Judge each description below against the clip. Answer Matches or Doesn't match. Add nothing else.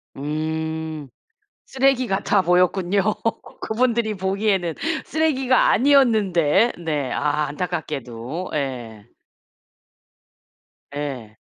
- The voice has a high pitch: Doesn't match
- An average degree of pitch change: Doesn't match